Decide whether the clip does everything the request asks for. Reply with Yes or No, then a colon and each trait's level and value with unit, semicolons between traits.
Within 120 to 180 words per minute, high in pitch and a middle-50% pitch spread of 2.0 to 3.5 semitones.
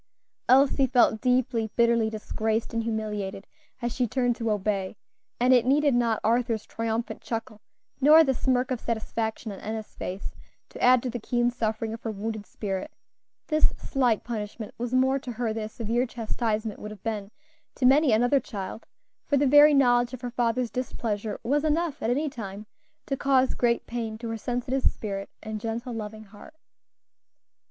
Yes: average, 175 wpm; high, 235 Hz; average, 2.7 semitones